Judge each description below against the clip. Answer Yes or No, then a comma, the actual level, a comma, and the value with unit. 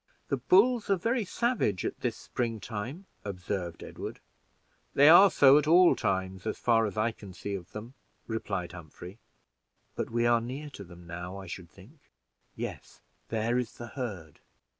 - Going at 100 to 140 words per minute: No, average, 170 wpm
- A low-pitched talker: Yes, low, 110 Hz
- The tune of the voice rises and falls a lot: Yes, wide, 6.7 semitones